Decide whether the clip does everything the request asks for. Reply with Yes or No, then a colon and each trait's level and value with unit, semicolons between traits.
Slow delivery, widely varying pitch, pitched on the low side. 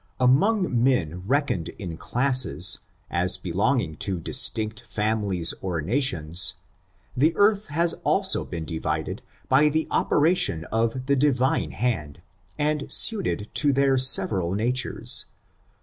Yes: slow, 120 wpm; wide, 7.5 semitones; low, 120 Hz